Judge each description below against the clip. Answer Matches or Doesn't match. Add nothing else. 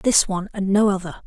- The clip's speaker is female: Matches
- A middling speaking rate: Doesn't match